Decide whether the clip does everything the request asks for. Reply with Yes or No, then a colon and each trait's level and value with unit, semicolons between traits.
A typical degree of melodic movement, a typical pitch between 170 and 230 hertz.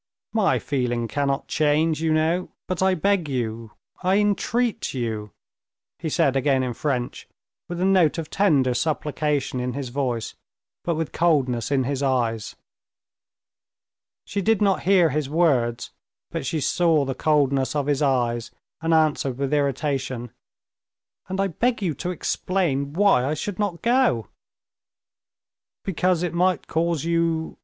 No: average, 4.9 semitones; medium, 150 Hz